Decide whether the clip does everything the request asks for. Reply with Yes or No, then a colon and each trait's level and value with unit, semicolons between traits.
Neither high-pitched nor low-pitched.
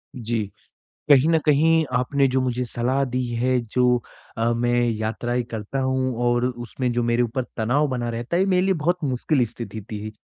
No: low, 125 Hz